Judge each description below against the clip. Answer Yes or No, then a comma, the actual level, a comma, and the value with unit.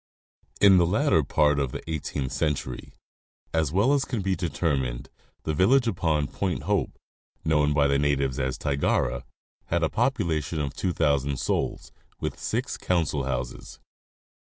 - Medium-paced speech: Yes, average, 150 wpm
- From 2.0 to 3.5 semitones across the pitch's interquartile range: No, average, 4.6 semitones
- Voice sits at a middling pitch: No, very low, 75 Hz